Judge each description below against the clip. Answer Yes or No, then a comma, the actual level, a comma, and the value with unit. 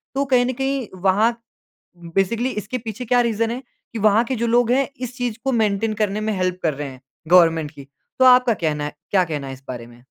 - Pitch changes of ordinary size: No, wide, 7.1 semitones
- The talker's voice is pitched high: Yes, high, 215 Hz